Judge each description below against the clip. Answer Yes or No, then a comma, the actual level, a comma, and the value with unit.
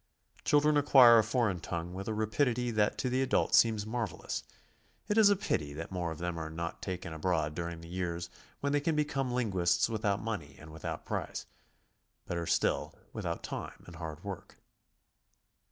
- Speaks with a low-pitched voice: Yes, low, 100 Hz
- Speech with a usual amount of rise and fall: No, wide, 6.5 semitones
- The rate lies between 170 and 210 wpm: Yes, average, 195 wpm